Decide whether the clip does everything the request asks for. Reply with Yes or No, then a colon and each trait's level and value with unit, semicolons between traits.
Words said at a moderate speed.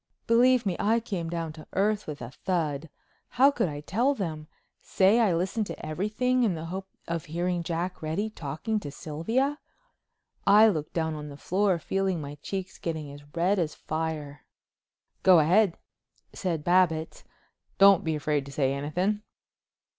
Yes: average, 160 wpm